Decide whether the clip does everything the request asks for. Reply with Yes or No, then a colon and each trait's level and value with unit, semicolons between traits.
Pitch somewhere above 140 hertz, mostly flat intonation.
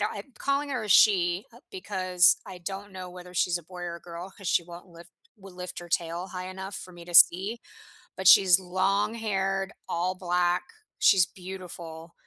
Yes: medium, 185 Hz; narrow, 1.9 semitones